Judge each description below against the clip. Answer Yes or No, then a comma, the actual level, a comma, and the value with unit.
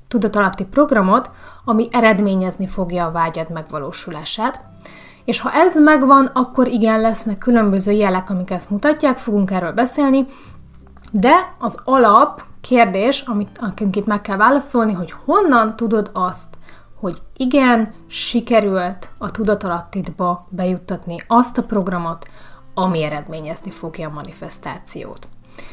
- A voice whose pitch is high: Yes, high, 210 Hz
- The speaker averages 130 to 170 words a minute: No, average, 115 wpm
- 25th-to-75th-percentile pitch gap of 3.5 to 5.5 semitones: Yes, average, 4.9 semitones